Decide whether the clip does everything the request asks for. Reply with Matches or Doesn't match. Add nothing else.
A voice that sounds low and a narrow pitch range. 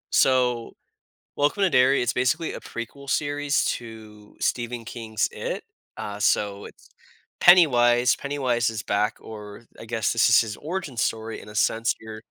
Doesn't match